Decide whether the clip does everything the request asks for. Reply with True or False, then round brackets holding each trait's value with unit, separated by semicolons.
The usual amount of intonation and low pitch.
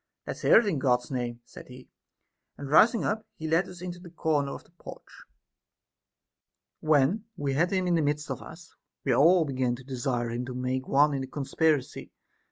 False (4.7 semitones; 145 Hz)